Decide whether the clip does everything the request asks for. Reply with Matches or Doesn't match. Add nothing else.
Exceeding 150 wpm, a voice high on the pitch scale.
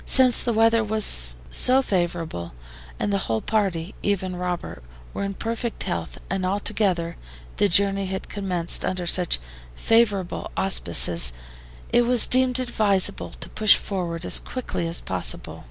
Doesn't match